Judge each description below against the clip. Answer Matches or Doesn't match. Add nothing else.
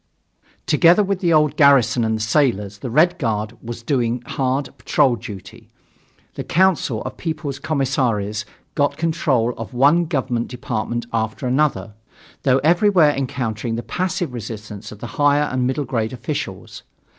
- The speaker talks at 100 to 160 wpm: Matches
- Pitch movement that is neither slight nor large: Matches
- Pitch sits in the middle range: Doesn't match